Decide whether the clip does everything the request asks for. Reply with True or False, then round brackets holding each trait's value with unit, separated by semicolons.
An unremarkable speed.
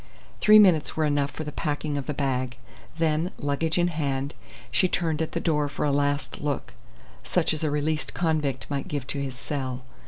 True (195 wpm)